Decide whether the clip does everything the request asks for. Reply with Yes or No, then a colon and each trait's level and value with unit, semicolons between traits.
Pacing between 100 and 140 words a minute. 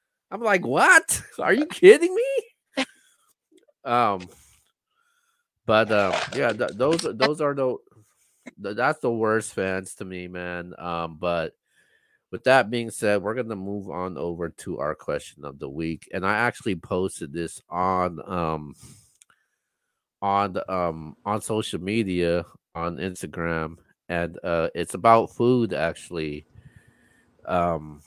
Yes: slow, 135 wpm